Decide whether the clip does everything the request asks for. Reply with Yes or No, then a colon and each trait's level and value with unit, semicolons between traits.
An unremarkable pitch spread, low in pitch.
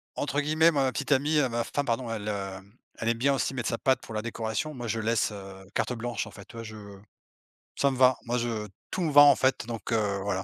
Yes: average, 3.9 semitones; low, 120 Hz